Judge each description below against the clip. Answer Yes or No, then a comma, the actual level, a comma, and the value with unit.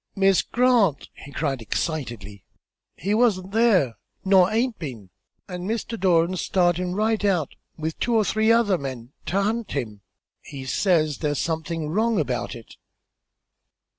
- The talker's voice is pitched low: No, medium, 180 Hz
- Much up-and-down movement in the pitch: Yes, wide, 6.8 semitones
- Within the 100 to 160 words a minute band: Yes, average, 140 wpm